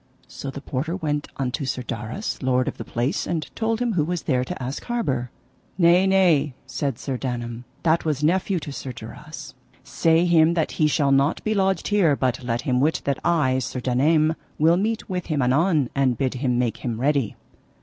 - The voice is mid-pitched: Yes, medium, 145 Hz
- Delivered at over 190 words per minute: Yes, average, 200 wpm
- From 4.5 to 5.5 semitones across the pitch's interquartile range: Yes, average, 4.9 semitones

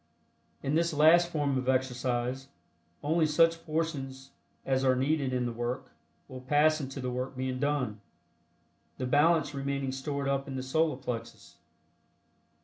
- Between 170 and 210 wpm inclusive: No, average, 145 wpm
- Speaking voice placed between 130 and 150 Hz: Yes, low, 135 Hz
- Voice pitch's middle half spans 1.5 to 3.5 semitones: Yes, average, 2.7 semitones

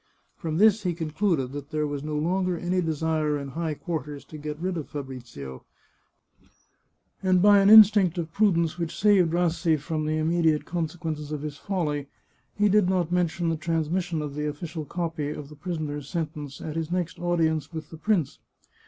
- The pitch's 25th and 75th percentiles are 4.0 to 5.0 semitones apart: No, average, 2.8 semitones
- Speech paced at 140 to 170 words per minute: No, average, 180 wpm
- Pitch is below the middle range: No, medium, 160 Hz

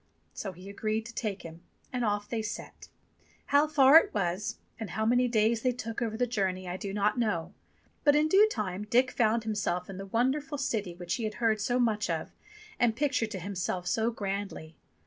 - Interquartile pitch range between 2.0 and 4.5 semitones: Yes, average, 3.9 semitones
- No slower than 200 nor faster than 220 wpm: Yes, fast, 205 wpm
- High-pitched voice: Yes, high, 215 Hz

